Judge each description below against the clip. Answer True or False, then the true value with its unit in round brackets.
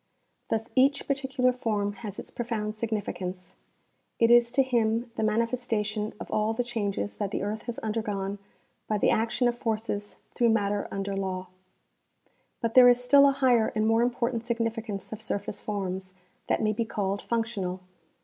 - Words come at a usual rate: True (170 wpm)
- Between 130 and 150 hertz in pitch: False (220 Hz)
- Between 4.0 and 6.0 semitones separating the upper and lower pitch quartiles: False (2.7 semitones)